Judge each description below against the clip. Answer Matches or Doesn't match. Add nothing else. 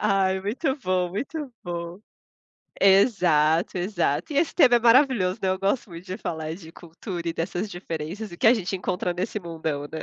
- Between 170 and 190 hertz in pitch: Matches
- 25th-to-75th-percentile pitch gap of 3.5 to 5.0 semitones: Matches